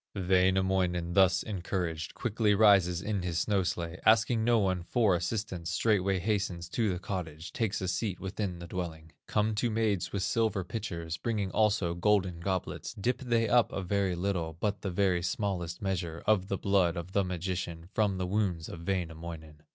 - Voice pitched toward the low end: Yes, very low, 95 Hz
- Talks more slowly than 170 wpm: No, average, 175 wpm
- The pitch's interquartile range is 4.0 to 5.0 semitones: No, average, 3.1 semitones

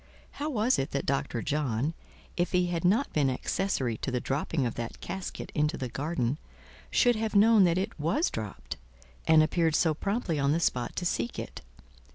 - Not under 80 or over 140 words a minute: No, average, 190 wpm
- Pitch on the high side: No, medium, 160 Hz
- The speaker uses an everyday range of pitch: No, wide, 6.1 semitones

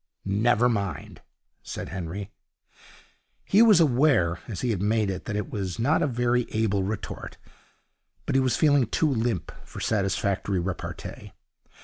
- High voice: No, low, 110 Hz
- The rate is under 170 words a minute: Yes, average, 140 wpm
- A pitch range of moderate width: Yes, average, 4.1 semitones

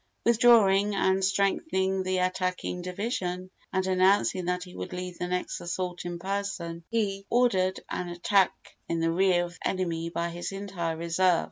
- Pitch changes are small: Yes, narrow, 1.8 semitones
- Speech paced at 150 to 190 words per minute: Yes, average, 160 wpm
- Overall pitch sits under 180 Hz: No, medium, 185 Hz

